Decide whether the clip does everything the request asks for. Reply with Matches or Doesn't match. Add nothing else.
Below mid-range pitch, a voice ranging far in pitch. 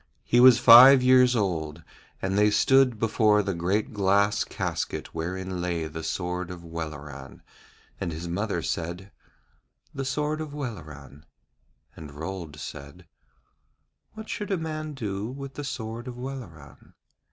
Matches